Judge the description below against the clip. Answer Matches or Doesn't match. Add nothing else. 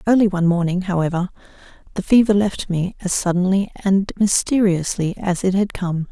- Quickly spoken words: Doesn't match